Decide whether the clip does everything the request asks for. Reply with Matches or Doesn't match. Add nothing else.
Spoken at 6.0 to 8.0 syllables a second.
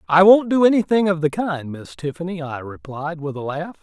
Doesn't match